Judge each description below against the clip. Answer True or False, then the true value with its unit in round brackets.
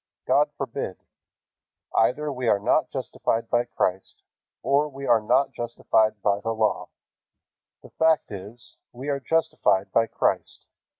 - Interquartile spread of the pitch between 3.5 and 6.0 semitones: True (4.3 semitones)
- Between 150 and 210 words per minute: False (135 wpm)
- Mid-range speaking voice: False (120 Hz)